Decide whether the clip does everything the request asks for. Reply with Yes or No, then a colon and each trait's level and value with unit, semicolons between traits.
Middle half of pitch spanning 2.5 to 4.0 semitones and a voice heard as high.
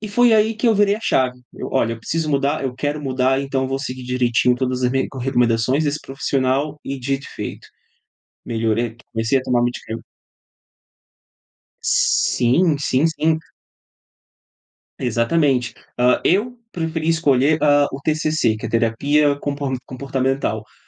No: average, 3.5 semitones; low, 135 Hz